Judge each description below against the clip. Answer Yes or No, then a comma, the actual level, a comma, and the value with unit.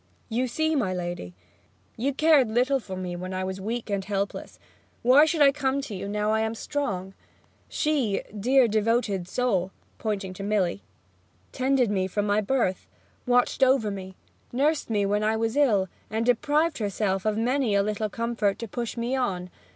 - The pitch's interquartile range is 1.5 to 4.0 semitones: No, average, 4.5 semitones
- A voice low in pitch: No, high, 220 Hz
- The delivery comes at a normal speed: Yes, average, 175 wpm